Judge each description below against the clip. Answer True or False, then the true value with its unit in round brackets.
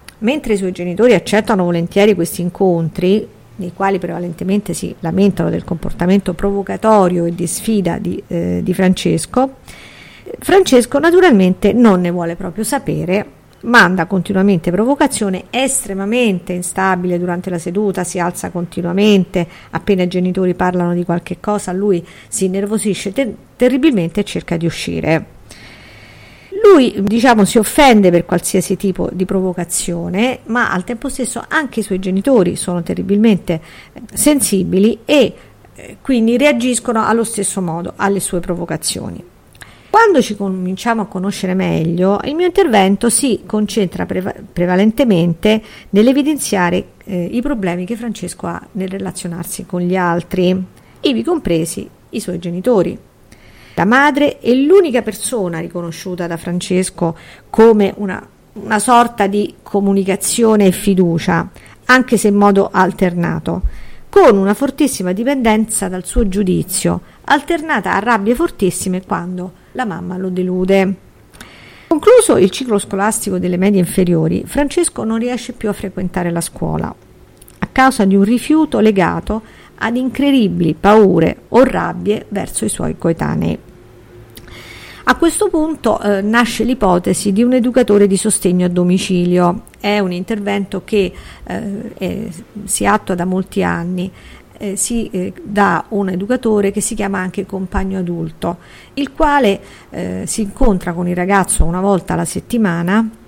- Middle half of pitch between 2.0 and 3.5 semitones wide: False (3.9 semitones)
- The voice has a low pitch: False (195 Hz)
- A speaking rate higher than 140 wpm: False (135 wpm)